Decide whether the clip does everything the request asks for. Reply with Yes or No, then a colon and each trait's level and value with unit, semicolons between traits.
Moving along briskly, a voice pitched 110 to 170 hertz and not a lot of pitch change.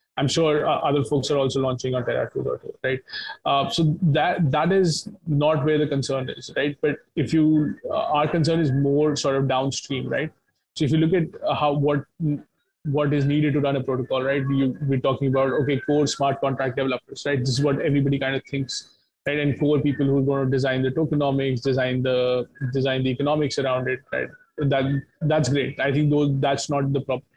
Yes: fast, 210 wpm; medium, 140 Hz; narrow, 2.0 semitones